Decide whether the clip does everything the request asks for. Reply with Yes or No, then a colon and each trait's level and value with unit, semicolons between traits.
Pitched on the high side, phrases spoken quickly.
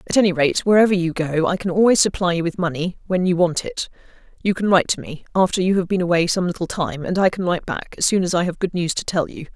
No: medium, 180 Hz; fast, 285 wpm